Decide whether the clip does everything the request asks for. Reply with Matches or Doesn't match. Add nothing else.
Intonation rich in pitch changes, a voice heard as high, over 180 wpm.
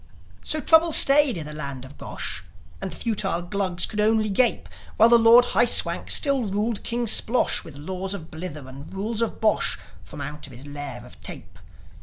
Matches